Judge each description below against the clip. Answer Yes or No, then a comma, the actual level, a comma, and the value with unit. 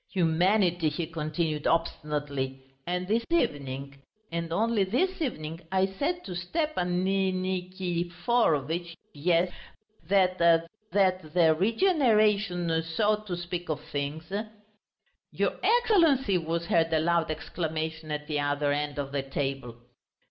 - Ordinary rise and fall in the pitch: Yes, average, 3.8 semitones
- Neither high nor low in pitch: Yes, medium, 170 Hz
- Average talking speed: No, slow, 125 wpm